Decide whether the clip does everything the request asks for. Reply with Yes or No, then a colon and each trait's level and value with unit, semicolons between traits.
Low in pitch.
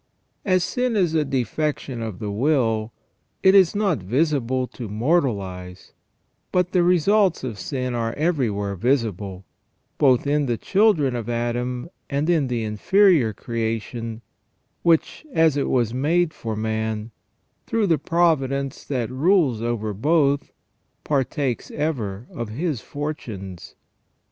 Yes: low, 130 Hz